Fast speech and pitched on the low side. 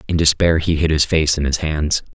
Yes: fast, 250 wpm; very low, 80 Hz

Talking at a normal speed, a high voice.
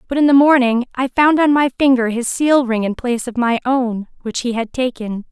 No: fast, 235 wpm; very high, 250 Hz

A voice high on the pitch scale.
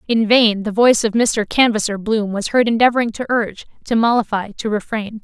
Yes: high, 220 Hz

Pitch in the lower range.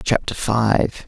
Yes: low, 110 Hz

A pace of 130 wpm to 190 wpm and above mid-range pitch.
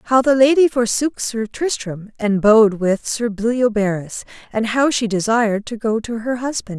Yes: average, 175 wpm; high, 230 Hz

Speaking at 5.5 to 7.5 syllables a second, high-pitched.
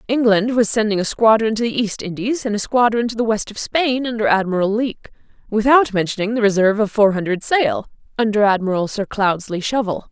Yes: 5.8 syllables/s; high, 215 Hz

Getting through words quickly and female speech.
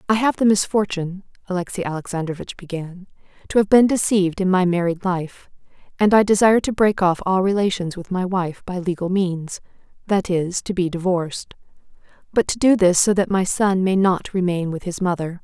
No: average, 185 wpm; female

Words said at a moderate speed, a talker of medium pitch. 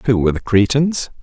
No: average, 195 wpm; low, 120 Hz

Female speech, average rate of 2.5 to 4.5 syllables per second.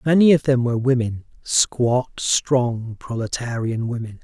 No: male; 4.2 syllables/s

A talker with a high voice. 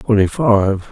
No: low, 105 Hz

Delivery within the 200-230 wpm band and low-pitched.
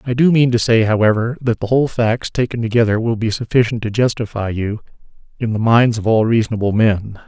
Yes: fast, 205 wpm; low, 115 Hz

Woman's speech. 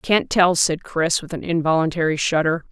Yes: female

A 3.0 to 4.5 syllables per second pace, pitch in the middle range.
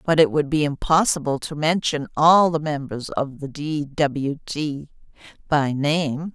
Yes: 4.0 syllables/s; medium, 150 Hz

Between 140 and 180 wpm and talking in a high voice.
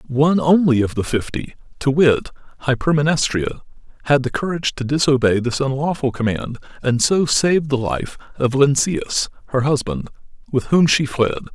No: average, 150 wpm; low, 135 Hz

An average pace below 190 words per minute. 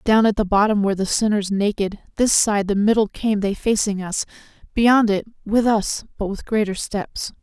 No: average, 195 wpm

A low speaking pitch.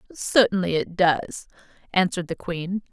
No: medium, 185 Hz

